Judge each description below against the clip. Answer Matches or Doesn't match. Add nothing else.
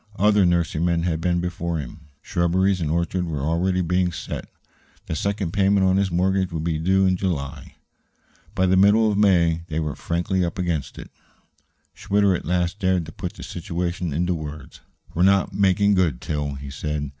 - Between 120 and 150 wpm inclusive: Doesn't match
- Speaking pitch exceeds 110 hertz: Doesn't match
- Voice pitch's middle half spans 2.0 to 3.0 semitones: Matches